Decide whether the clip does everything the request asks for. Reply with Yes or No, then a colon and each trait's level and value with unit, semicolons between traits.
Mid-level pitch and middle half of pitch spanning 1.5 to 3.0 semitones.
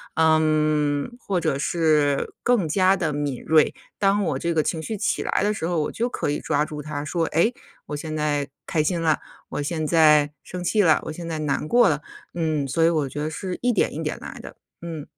Yes: medium, 155 Hz; average, 2.7 semitones